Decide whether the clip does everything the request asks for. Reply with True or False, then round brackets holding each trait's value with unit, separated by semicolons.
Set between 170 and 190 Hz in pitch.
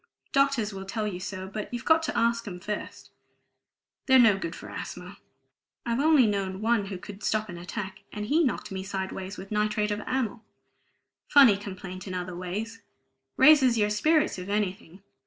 False (210 Hz)